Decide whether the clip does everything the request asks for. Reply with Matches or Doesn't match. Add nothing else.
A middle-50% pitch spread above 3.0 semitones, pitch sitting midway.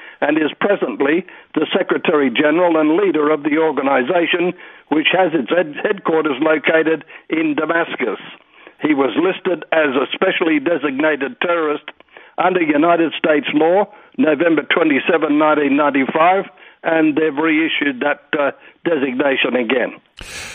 Doesn't match